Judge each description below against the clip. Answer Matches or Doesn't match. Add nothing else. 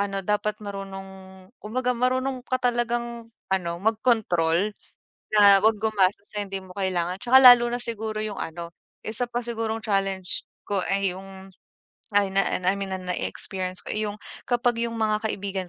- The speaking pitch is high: Matches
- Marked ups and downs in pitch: Doesn't match